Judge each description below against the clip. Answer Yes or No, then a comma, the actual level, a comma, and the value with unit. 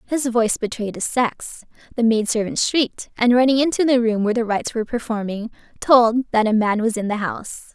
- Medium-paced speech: No, fast, 210 wpm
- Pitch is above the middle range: Yes, high, 230 Hz